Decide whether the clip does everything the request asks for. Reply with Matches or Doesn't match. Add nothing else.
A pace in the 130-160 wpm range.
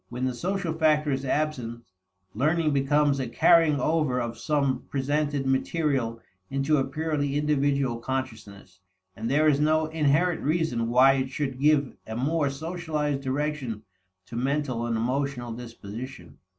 Matches